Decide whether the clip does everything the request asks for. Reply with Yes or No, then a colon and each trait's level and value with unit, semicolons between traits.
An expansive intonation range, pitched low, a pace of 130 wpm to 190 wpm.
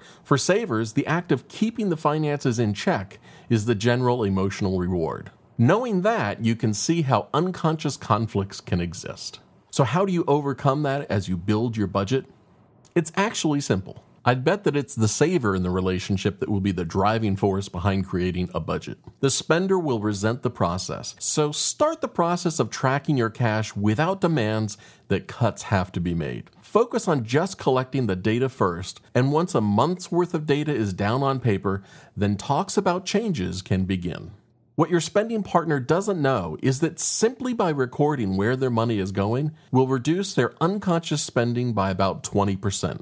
Yes: wide, 7.7 semitones; low, 125 Hz; average, 180 wpm